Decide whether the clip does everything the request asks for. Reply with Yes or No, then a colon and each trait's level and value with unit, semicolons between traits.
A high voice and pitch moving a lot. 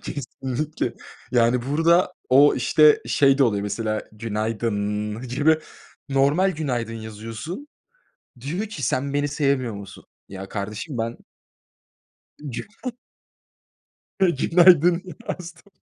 No: low, 135 Hz; wide, 5.7 semitones